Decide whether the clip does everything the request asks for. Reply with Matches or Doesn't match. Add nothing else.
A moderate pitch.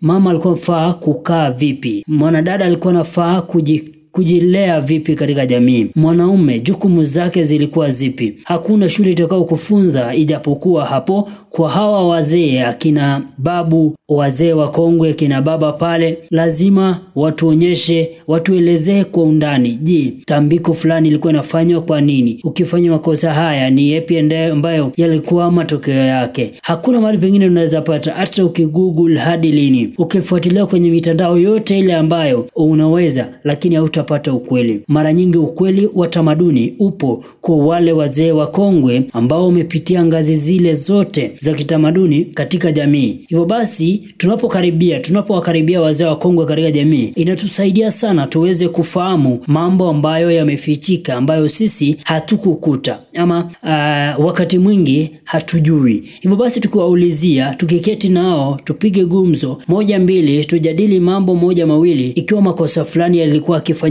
Matches